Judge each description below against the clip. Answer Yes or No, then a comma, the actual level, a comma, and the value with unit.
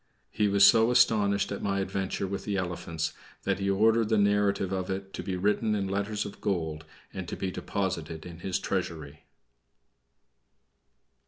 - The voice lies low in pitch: Yes, low, 100 Hz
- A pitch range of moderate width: No, narrow, 2.0 semitones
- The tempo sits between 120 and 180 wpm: Yes, average, 165 wpm